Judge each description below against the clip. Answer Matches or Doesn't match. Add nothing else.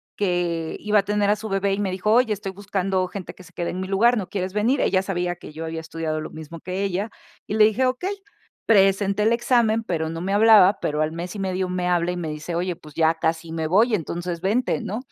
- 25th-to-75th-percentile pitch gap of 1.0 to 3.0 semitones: Doesn't match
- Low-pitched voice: Doesn't match